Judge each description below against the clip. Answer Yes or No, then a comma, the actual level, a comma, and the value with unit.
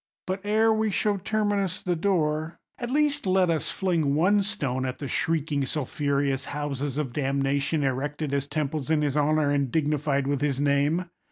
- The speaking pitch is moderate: Yes, medium, 150 Hz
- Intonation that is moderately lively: Yes, average, 4.7 semitones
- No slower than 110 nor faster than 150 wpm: No, average, 170 wpm